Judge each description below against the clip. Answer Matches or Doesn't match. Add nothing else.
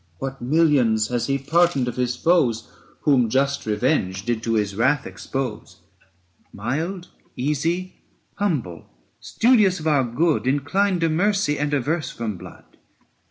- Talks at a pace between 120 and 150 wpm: Matches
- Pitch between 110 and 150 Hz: Matches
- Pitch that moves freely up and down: Matches